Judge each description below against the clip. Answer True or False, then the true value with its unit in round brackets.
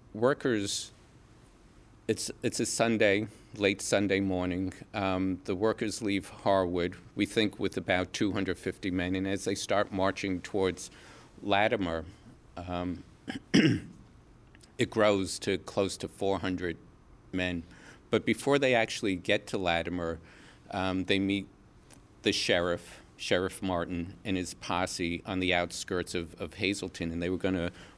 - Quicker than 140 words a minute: False (135 wpm)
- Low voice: True (95 Hz)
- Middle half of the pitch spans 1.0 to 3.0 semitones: True (2.4 semitones)